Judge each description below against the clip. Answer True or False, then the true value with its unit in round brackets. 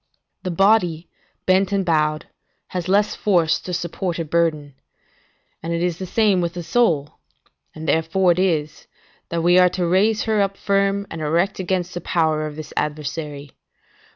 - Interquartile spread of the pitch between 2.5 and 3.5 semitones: True (3.2 semitones)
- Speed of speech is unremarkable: True (170 wpm)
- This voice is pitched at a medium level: True (175 Hz)